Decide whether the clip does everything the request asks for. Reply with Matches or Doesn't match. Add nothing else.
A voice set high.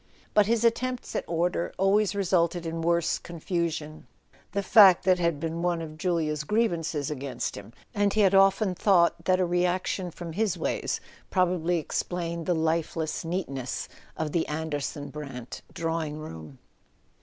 Doesn't match